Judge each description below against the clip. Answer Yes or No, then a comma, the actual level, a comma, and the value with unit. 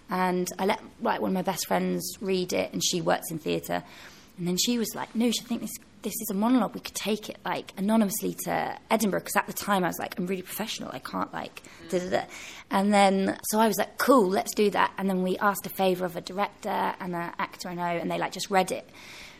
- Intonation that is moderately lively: Yes, average, 3.1 semitones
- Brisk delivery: Yes, fast, 250 wpm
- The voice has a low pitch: No, high, 195 Hz